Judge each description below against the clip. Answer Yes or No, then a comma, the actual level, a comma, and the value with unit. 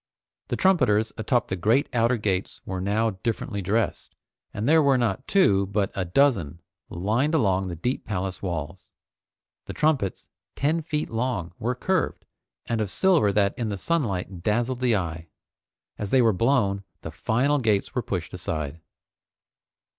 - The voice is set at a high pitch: No, low, 110 Hz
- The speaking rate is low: No, average, 155 wpm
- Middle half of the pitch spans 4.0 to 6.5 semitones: Yes, average, 5.0 semitones